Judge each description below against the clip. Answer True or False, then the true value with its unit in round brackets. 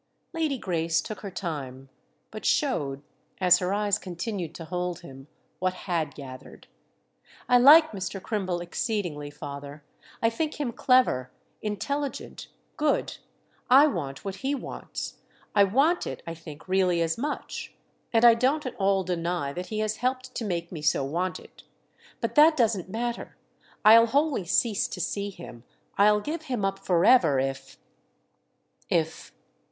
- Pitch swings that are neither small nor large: False (6.4 semitones)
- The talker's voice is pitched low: False (195 Hz)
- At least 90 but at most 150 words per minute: True (145 wpm)